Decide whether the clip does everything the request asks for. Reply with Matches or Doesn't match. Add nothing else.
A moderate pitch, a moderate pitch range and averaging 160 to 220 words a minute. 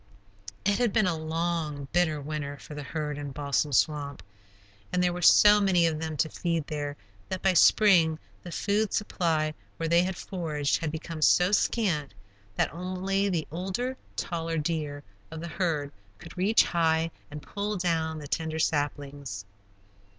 Matches